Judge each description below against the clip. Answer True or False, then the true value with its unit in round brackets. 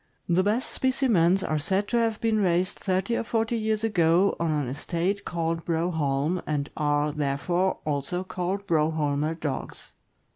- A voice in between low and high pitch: True (175 Hz)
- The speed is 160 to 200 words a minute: False (150 wpm)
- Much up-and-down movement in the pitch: False (4.7 semitones)